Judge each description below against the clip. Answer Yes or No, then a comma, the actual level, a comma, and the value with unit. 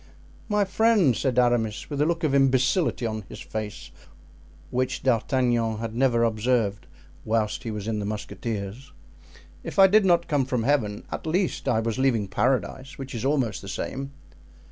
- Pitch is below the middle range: Yes, low, 125 Hz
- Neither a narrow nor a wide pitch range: Yes, average, 4.0 semitones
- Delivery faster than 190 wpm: No, average, 165 wpm